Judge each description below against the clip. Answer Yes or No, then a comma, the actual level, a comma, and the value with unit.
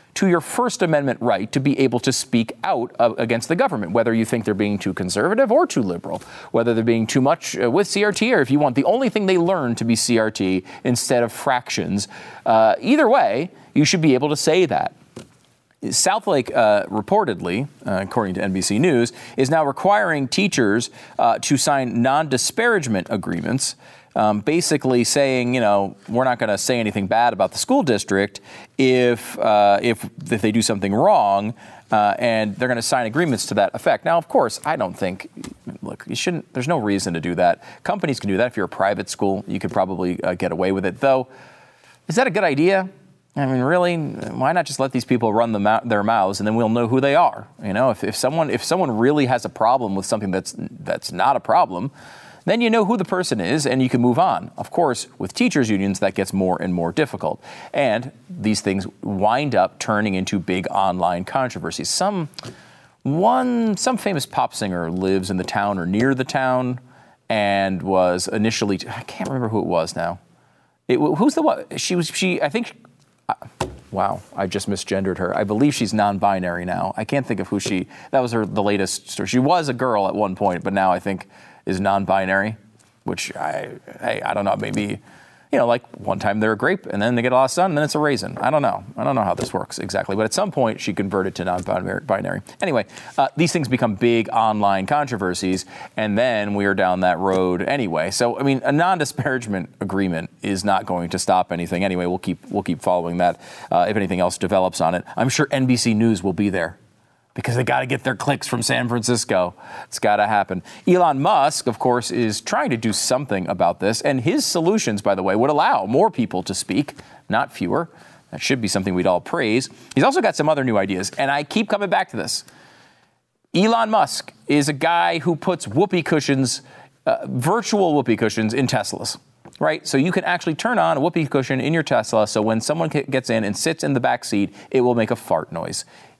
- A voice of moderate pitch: No, low, 115 Hz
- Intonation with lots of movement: Yes, wide, 6.2 semitones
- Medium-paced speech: No, fast, 215 wpm